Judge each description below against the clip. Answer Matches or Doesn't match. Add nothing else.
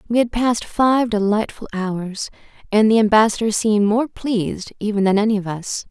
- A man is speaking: Doesn't match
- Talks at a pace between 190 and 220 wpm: Doesn't match